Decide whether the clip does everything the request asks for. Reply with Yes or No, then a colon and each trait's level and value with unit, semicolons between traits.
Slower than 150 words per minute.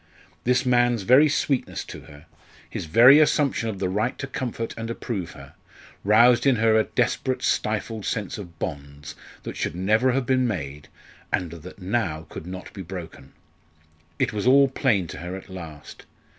No: average, 170 wpm